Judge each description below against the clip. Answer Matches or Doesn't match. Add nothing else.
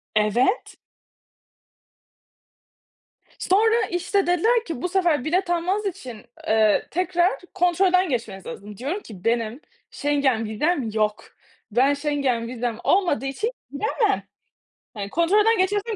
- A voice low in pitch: Doesn't match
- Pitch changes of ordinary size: Doesn't match